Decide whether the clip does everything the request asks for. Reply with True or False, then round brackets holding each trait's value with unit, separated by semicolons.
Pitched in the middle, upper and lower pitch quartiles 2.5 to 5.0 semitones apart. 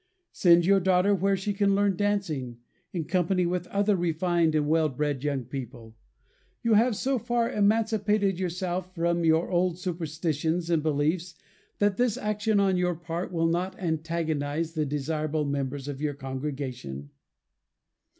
True (170 Hz; 4.3 semitones)